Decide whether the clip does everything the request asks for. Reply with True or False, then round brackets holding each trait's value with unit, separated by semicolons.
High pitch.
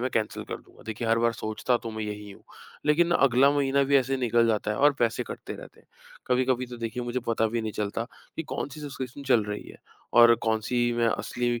False (120 Hz)